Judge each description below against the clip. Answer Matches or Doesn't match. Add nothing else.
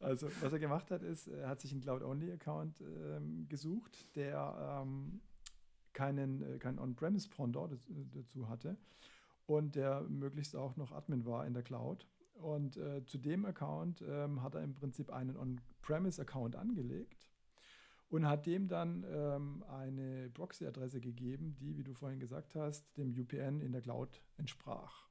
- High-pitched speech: Doesn't match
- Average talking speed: Matches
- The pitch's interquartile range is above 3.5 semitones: Doesn't match